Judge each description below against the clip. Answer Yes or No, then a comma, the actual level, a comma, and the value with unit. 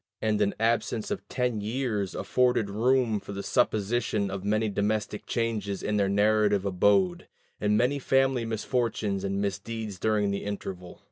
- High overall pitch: No, low, 105 Hz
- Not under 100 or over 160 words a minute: Yes, average, 150 wpm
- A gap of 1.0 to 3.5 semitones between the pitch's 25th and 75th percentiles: Yes, narrow, 2.4 semitones